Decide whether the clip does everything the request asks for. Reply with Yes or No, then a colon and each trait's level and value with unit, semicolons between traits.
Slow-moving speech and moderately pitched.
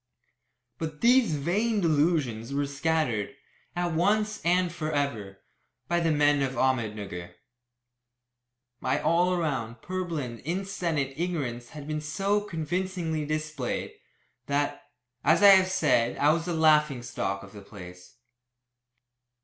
Yes: slow, 125 wpm; medium, 155 Hz